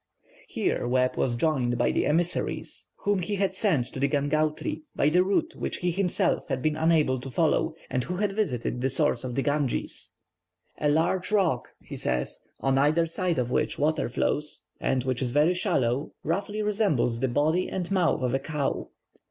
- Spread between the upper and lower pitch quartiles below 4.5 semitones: No, wide, 5.5 semitones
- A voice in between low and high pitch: Yes, medium, 150 Hz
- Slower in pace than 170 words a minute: No, average, 185 wpm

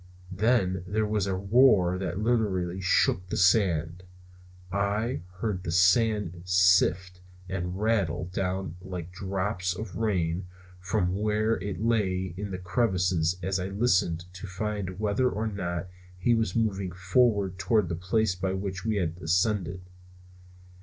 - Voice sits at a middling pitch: No, very low, 95 Hz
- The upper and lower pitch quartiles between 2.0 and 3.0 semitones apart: Yes, average, 2.7 semitones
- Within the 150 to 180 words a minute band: No, average, 140 wpm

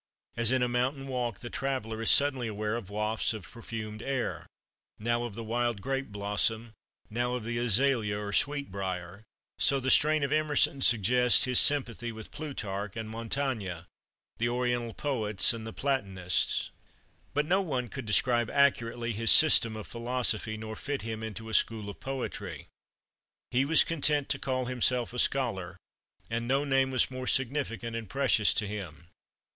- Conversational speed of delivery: Yes, average, 165 wpm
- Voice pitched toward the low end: Yes, low, 120 Hz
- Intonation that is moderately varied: Yes, average, 3.6 semitones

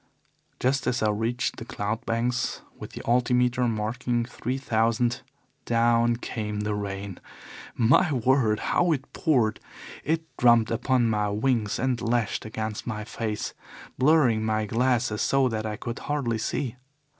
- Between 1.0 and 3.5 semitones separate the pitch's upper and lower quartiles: Yes, narrow, 2.5 semitones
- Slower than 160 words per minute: Yes, average, 145 wpm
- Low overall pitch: Yes, low, 115 Hz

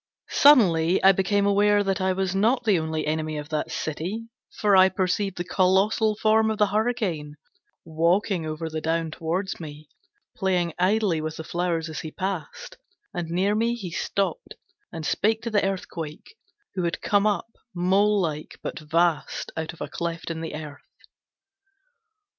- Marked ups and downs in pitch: No, average, 4.1 semitones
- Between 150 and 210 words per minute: Yes, average, 165 wpm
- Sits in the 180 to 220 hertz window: Yes, medium, 185 Hz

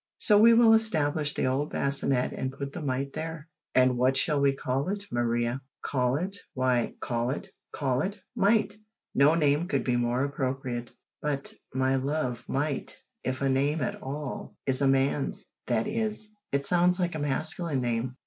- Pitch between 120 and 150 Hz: Yes, medium, 140 Hz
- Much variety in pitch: No, average, 3.7 semitones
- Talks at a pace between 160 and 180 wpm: Yes, average, 175 wpm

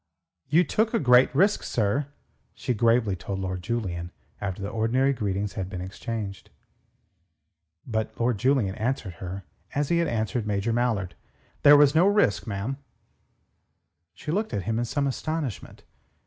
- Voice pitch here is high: No, low, 115 Hz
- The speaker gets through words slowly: No, average, 150 wpm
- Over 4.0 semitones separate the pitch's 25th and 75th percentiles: Yes, wide, 5.6 semitones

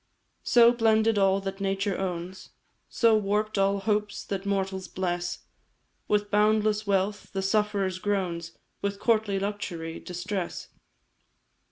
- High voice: Yes, high, 200 Hz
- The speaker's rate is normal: No, slow, 120 wpm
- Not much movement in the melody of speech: Yes, narrow, 1.8 semitones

